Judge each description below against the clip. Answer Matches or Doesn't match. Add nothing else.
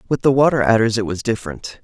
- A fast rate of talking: Matches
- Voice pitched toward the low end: Matches